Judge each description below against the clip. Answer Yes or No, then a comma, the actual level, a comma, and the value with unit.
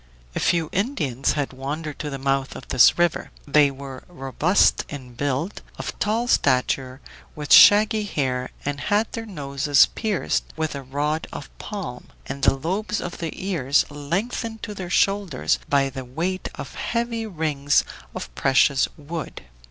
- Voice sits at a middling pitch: Yes, medium, 150 Hz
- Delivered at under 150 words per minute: No, average, 155 wpm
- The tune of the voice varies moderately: No, wide, 6.0 semitones